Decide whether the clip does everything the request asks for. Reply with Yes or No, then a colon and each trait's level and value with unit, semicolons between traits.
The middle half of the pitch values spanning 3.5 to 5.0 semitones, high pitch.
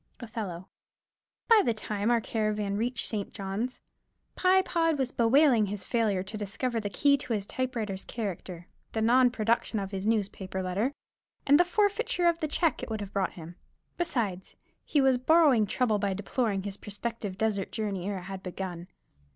Yes: average, 4.5 semitones; high, 220 Hz